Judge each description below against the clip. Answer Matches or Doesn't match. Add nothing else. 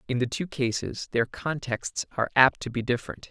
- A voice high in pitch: Doesn't match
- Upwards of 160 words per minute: Matches